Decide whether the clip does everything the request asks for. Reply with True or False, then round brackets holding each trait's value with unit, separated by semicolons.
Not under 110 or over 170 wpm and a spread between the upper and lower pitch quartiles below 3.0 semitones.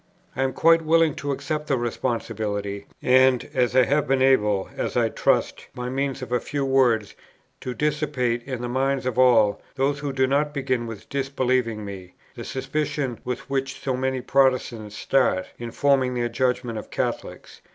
False (180 wpm; 2.5 semitones)